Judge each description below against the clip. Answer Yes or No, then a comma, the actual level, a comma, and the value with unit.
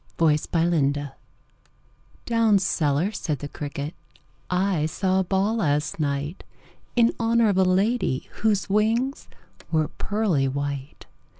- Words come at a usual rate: No, slow, 125 wpm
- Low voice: No, medium, 180 Hz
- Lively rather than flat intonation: Yes, wide, 6.4 semitones